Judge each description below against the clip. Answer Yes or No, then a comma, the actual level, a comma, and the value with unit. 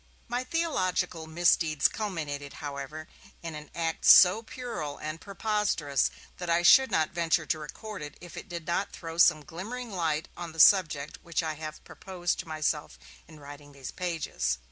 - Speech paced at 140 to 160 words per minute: No, average, 170 wpm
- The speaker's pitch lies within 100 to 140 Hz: No, medium, 165 Hz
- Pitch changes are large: No, average, 3.3 semitones